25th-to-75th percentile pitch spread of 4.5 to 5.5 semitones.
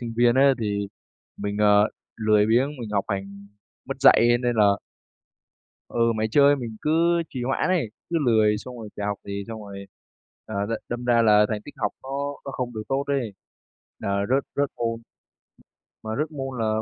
No: average, 4.1 semitones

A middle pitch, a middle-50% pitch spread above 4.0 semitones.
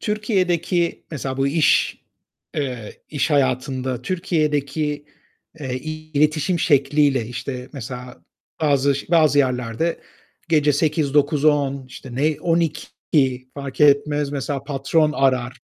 No: medium, 145 Hz; average, 2.7 semitones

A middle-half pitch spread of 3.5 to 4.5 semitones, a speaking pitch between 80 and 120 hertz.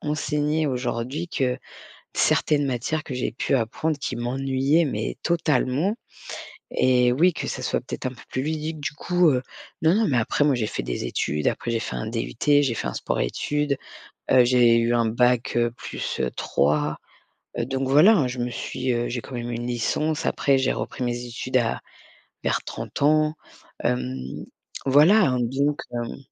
No: average, 3.8 semitones; low, 130 Hz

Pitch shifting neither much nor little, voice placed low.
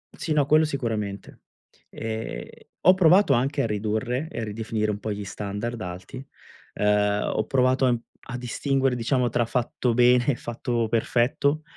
Yes: average, 3.7 semitones; low, 120 Hz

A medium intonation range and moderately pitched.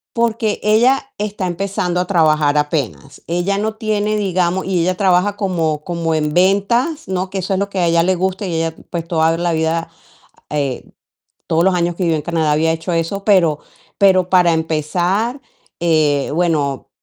Yes: average, 3.4 semitones; medium, 175 Hz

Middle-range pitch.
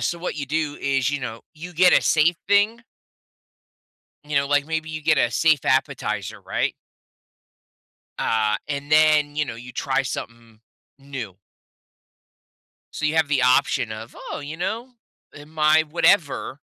Yes: medium, 145 Hz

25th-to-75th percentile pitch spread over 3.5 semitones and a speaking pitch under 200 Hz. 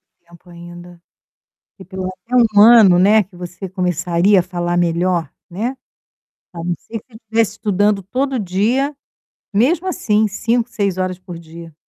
Yes: average, 3.9 semitones; medium, 185 Hz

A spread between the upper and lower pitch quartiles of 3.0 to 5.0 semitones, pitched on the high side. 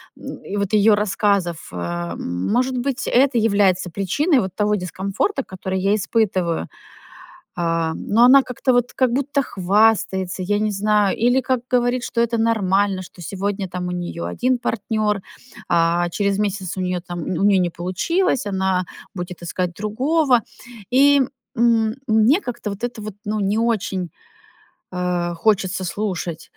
Yes: average, 4.2 semitones; high, 205 Hz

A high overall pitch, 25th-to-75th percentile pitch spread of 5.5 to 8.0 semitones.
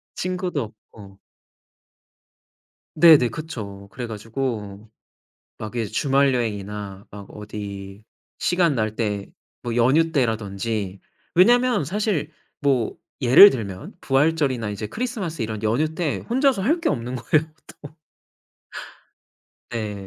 No: low, 120 Hz; wide, 7.3 semitones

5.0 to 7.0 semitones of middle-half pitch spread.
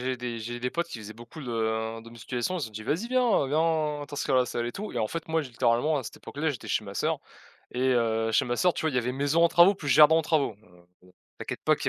Yes: wide, 5.4 semitones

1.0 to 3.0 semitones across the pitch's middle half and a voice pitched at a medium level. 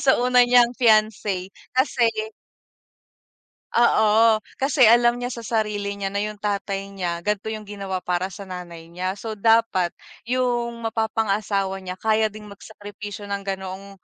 No: average, 2.7 semitones; high, 210 Hz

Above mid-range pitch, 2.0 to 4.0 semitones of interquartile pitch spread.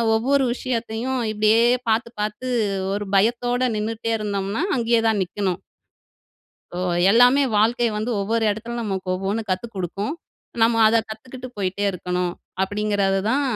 Yes: high, 220 Hz; average, 3.0 semitones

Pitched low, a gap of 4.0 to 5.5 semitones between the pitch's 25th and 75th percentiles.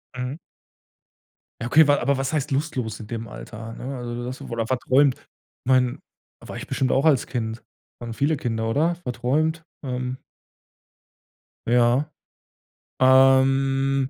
No: low, 130 Hz; narrow, 2.4 semitones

